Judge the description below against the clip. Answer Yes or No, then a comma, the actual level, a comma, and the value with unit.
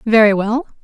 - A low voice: No, high, 225 Hz